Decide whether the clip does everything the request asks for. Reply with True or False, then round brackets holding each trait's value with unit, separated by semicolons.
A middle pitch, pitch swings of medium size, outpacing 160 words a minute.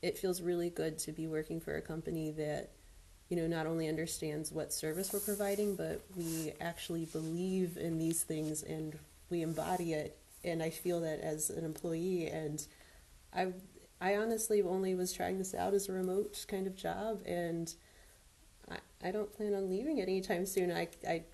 True (170 Hz; 3.3 semitones; 180 wpm)